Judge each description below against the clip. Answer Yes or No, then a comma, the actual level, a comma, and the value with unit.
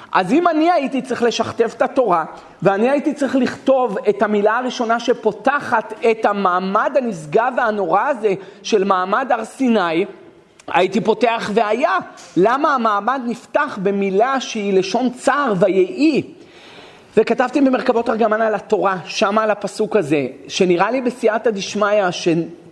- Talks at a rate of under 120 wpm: No, average, 130 wpm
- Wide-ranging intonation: No, average, 4.2 semitones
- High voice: Yes, high, 225 Hz